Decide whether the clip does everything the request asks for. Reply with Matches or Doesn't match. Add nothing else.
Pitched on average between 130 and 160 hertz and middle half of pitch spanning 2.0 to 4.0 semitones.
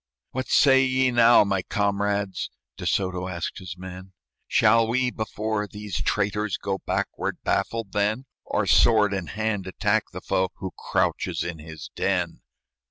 Doesn't match